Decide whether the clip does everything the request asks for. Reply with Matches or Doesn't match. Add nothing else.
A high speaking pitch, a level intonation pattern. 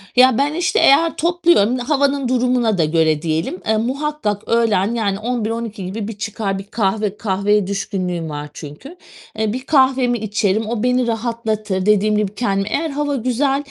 Doesn't match